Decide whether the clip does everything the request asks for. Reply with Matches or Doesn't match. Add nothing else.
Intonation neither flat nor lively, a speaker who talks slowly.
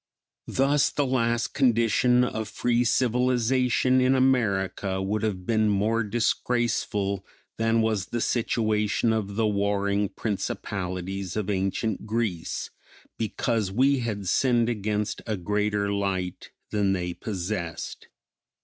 Matches